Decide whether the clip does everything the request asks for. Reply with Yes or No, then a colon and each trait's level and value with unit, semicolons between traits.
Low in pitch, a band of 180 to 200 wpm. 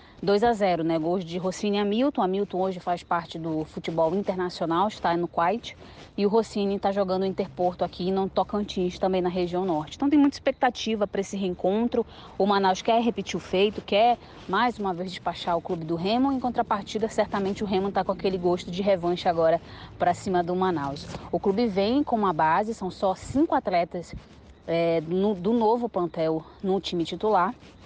No: high, 190 Hz; fast, 185 wpm